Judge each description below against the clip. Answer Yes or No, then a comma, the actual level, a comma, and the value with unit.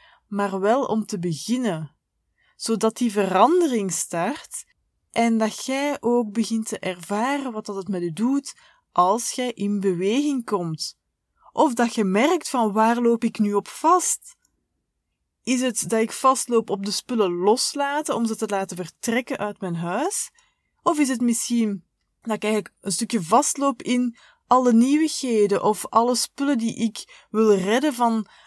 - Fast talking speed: No, average, 160 wpm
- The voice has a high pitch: Yes, high, 230 Hz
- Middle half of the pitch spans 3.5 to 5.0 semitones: Yes, average, 4.2 semitones